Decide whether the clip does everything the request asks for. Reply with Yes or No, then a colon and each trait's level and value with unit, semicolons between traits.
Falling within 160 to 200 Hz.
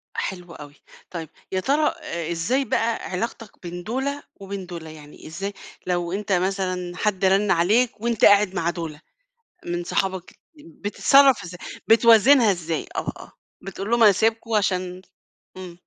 Yes: high, 190 Hz